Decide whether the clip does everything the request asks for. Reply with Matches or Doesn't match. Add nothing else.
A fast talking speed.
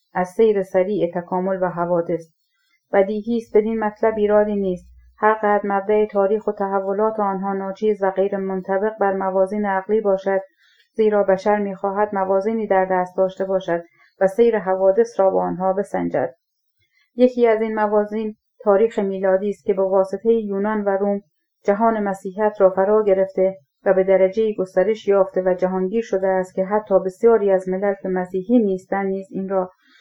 Matches